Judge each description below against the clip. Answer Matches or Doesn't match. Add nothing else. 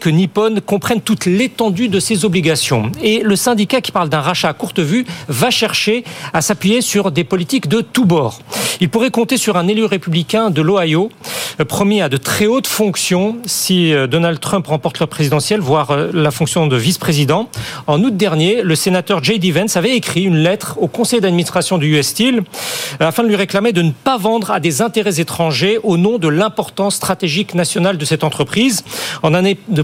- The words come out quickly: Doesn't match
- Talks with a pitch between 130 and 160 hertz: Doesn't match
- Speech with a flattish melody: Doesn't match